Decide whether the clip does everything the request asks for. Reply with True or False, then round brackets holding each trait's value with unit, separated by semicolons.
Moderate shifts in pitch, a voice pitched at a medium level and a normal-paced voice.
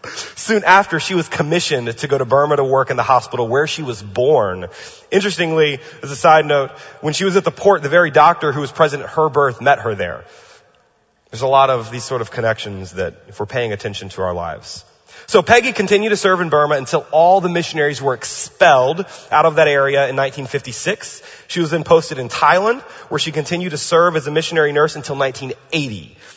False (3.8 semitones; 150 Hz; 210 wpm)